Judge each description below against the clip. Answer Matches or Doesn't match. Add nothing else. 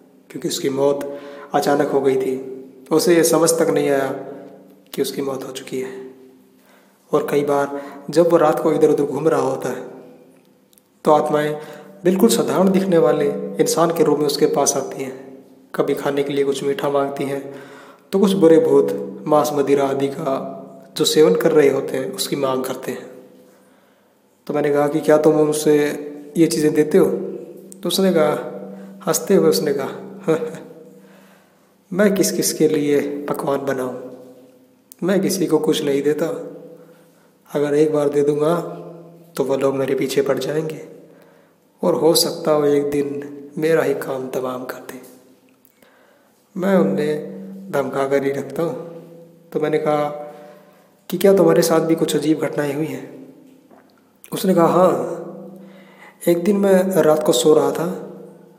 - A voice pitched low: Doesn't match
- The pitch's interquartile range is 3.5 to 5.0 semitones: Doesn't match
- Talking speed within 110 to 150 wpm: Doesn't match